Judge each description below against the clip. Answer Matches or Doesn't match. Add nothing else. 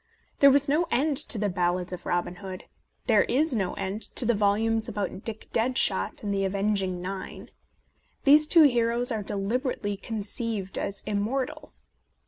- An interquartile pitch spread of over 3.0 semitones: Matches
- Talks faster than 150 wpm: Matches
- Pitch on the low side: Doesn't match